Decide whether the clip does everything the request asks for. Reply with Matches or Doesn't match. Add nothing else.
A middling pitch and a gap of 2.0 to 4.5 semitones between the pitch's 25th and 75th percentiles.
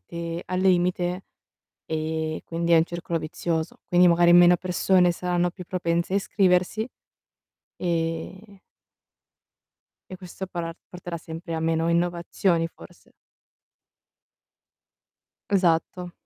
Doesn't match